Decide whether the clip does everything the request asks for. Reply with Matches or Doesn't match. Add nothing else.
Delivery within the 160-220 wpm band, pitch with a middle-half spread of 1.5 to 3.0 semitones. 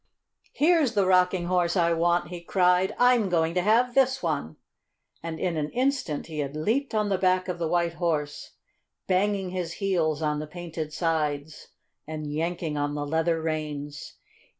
Doesn't match